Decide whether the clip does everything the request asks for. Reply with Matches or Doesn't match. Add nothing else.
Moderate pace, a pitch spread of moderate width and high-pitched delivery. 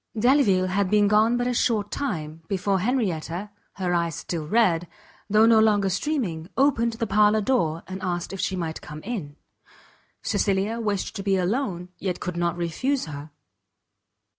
Matches